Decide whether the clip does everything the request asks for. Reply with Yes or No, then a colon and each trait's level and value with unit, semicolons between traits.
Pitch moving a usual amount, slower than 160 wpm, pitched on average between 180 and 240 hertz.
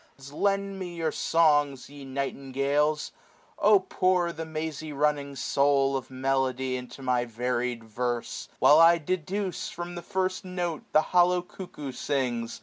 No: average, 4.7 semitones; average, 145 wpm; medium, 150 Hz